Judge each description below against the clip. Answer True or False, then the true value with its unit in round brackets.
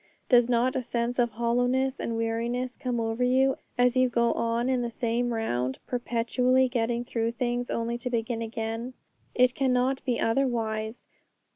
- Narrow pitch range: True (1.6 semitones)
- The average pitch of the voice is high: True (240 Hz)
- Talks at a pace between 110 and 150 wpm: False (160 wpm)